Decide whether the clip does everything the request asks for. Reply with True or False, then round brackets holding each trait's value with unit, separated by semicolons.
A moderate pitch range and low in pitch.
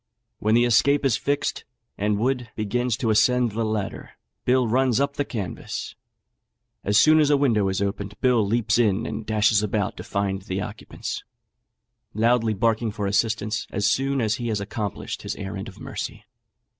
True (3.2 semitones; 110 Hz)